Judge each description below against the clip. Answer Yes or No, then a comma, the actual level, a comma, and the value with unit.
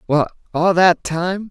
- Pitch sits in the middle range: Yes, medium, 175 Hz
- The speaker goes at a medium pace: Yes, average, 160 wpm